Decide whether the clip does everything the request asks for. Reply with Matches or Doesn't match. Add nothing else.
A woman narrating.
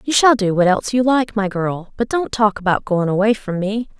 Matches